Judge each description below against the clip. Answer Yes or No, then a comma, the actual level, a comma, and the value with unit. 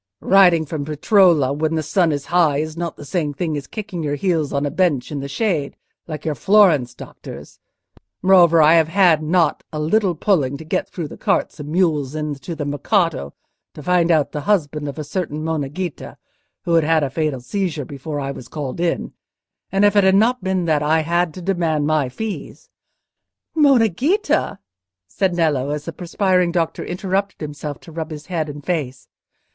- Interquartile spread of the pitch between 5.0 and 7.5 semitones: No, average, 3.7 semitones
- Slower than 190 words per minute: No, average, 195 wpm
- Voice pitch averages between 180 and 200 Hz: No, medium, 160 Hz